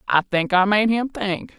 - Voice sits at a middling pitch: No, high, 205 Hz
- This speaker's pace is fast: Yes, fast, 225 wpm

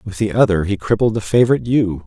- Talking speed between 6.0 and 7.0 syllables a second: Yes, 6.6 syllables/s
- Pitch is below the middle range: Yes, low, 100 Hz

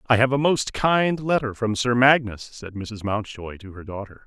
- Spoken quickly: Yes, fast, 210 wpm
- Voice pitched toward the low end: Yes, low, 120 Hz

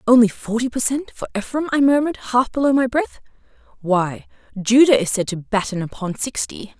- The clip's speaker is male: No, female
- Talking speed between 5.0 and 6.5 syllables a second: Yes, 5.5 syllables/s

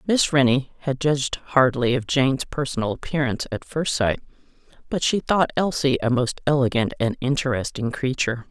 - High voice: No, low, 135 Hz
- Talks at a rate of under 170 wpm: Yes, average, 155 wpm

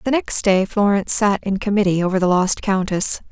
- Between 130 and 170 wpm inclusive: No, average, 200 wpm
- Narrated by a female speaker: Yes, female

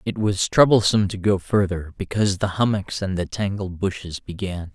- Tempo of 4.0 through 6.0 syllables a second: Yes, 5.3 syllables/s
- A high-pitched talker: No, very low, 95 Hz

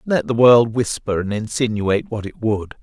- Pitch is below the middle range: Yes, low, 115 Hz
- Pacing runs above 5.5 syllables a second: No, 5.0 syllables/s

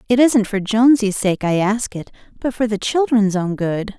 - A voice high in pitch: Yes, high, 215 Hz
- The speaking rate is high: Yes, fast, 210 wpm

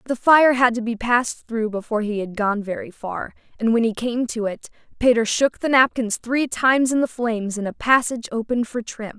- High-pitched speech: Yes, high, 235 Hz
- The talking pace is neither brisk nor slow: No, fast, 220 wpm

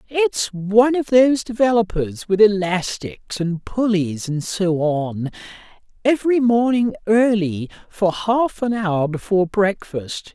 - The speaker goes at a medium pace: No, slow, 120 wpm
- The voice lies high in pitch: Yes, high, 205 Hz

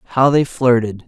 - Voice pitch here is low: Yes, low, 125 Hz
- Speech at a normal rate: Yes, average, 170 wpm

